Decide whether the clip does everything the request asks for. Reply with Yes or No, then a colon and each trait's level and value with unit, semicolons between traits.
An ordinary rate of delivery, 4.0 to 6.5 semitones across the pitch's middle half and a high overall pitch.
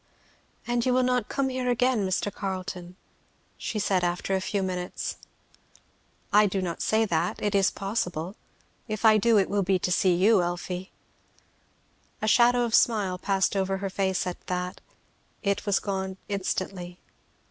No: average, 165 wpm; average, 2.9 semitones; high, 195 Hz